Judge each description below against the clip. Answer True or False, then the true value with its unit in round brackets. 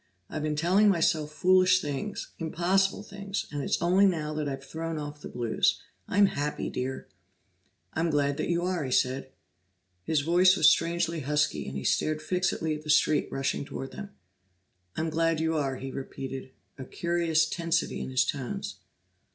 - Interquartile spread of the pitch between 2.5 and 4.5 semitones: True (3.5 semitones)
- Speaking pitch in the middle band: True (155 Hz)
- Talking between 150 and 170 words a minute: True (165 wpm)